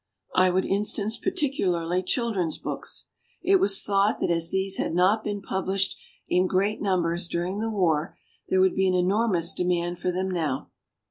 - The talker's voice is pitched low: No, high, 190 Hz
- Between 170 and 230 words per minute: Yes, average, 175 wpm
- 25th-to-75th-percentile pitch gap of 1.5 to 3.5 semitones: Yes, narrow, 2.4 semitones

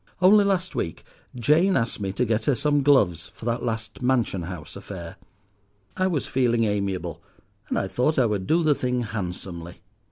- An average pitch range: No, wide, 6.9 semitones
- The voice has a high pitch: No, low, 115 Hz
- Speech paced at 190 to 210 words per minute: No, average, 180 wpm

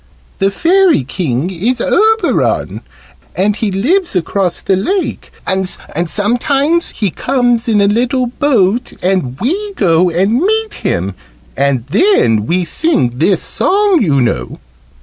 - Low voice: No, high, 205 Hz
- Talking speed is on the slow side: Yes, slow, 130 wpm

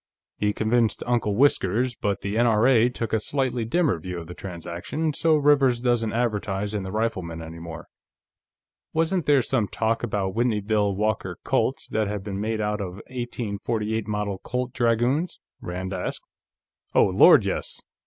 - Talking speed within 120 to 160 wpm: Yes, average, 155 wpm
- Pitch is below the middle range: Yes, low, 110 Hz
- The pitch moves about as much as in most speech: Yes, average, 3.6 semitones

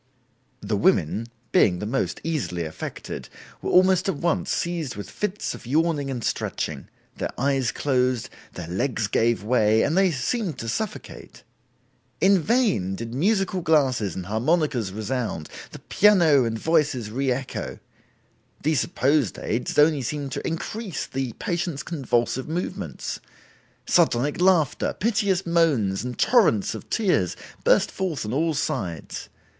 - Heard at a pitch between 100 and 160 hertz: Yes, medium, 140 Hz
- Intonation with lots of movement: Yes, wide, 6.8 semitones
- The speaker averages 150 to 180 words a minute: No, average, 140 wpm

